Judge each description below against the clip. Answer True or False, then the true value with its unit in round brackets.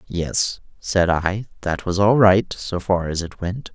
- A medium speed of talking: True (190 wpm)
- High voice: False (95 Hz)